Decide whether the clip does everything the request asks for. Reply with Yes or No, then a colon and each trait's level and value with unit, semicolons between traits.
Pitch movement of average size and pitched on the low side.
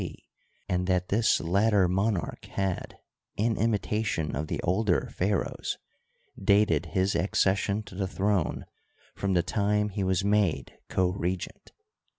No: narrow, 2.3 semitones; very low, 95 Hz